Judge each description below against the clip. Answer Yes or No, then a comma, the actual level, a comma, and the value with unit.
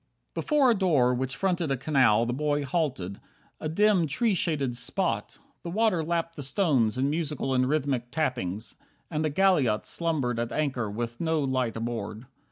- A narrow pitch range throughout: No, average, 5.3 semitones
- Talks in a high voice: No, medium, 140 Hz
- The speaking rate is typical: Yes, average, 175 wpm